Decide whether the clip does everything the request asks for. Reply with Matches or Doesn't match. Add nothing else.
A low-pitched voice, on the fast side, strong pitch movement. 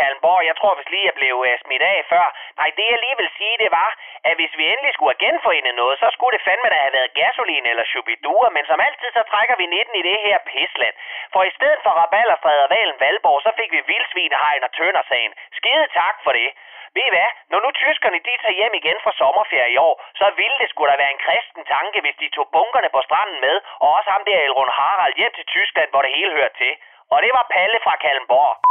Doesn't match